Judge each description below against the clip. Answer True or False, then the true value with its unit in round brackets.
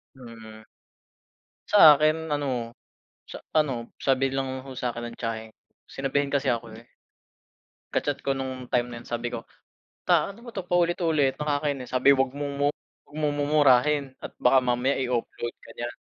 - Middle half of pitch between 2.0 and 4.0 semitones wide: True (3.2 semitones)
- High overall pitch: False (135 Hz)